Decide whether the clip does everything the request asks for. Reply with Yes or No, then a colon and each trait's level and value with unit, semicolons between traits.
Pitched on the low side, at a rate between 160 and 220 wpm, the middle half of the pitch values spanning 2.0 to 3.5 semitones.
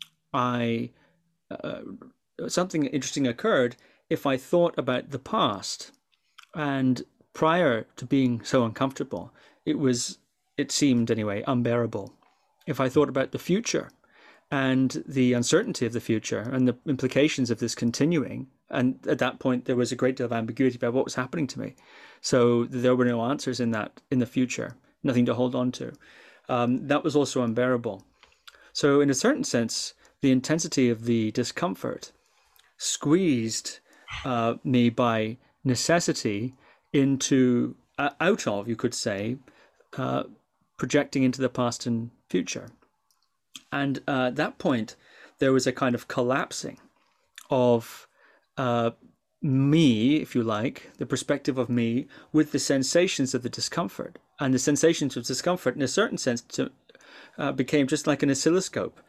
No: low, 130 Hz; average, 150 wpm; average, 3.0 semitones